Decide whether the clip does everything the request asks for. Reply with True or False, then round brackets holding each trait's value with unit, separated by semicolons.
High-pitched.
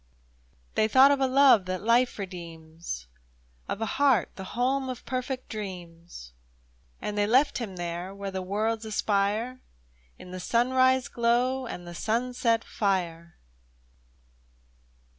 True (215 Hz)